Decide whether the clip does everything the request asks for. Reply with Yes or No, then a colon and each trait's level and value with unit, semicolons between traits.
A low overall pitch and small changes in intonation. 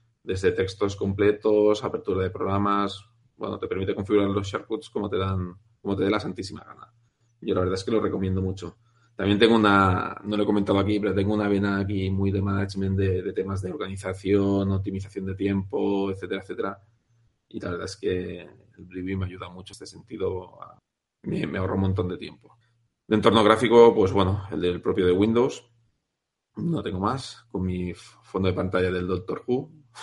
Yes: low, 100 Hz; narrow, 2.2 semitones